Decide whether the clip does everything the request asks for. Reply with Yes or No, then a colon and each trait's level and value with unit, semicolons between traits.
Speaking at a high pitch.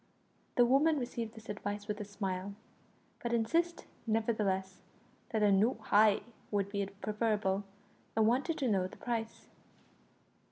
Yes: high, 215 Hz